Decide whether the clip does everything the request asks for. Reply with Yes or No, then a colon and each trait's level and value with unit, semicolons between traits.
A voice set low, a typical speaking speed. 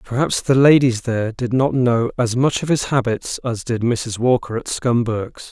Yes: low, 120 Hz; average, 195 wpm